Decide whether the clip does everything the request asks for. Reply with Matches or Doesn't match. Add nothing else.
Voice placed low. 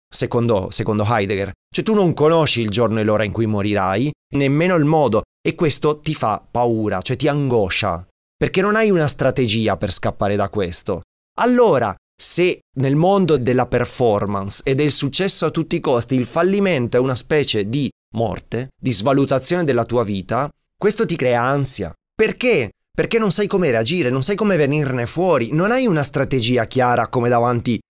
Matches